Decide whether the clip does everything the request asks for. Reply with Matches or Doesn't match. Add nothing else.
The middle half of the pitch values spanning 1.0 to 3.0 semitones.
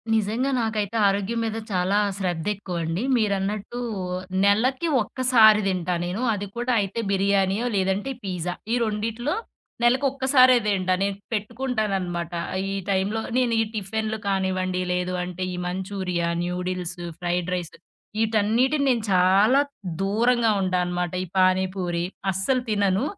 Doesn't match